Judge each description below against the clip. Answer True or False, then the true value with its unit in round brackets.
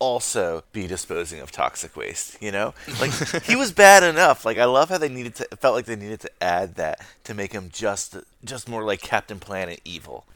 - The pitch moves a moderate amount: False (6.3 semitones)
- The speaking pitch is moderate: False (110 Hz)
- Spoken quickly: True (215 wpm)